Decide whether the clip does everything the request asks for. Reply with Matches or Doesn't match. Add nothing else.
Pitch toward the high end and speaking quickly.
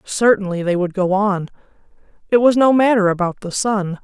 Doesn't match